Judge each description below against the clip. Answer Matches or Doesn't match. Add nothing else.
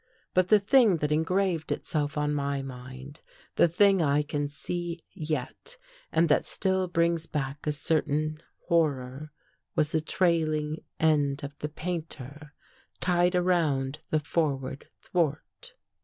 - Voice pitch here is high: Doesn't match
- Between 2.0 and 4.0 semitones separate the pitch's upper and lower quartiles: Matches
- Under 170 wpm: Matches